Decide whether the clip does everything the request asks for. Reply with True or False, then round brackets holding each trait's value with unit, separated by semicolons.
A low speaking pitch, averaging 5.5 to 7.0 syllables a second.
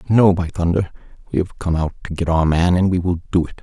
True (85 Hz; 6.1 syllables/s)